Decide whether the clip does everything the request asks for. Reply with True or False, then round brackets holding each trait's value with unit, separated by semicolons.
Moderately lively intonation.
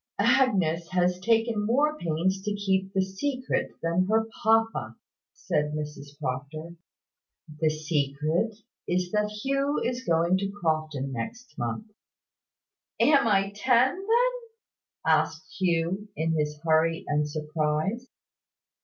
False (6.2 semitones)